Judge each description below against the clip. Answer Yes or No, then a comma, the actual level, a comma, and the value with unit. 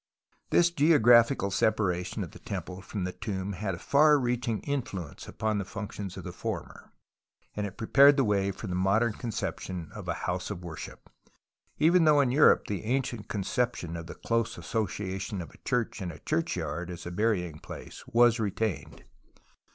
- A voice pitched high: No, low, 105 Hz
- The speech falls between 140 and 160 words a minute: No, average, 175 wpm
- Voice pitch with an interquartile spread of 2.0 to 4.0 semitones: No, average, 4.7 semitones